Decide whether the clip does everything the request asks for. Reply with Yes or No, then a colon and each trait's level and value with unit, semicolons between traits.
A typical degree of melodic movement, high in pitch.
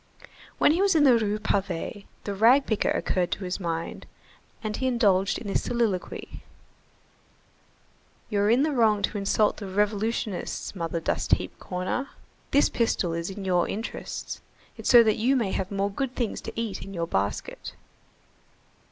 Yes: average, 3.6 semitones; high, 205 Hz